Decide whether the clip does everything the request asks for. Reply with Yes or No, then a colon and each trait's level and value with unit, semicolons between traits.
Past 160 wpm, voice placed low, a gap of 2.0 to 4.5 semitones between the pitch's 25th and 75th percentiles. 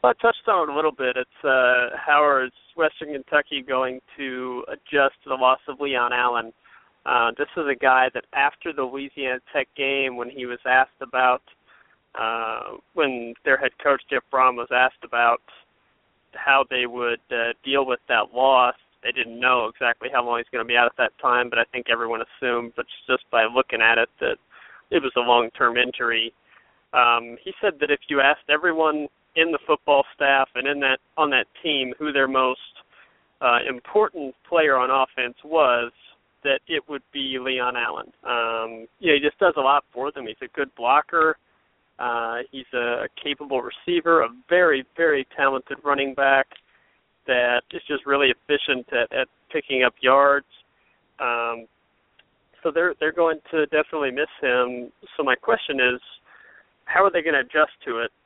Yes: average, 180 wpm; low, 130 Hz; average, 2.8 semitones